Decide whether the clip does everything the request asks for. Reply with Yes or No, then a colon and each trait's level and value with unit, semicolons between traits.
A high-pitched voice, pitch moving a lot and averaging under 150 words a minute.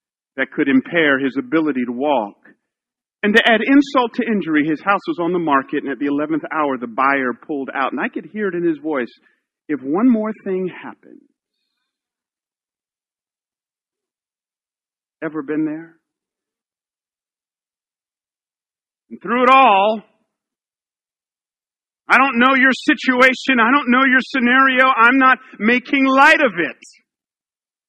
Yes: high, 210 Hz; wide, 9.0 semitones; average, 140 wpm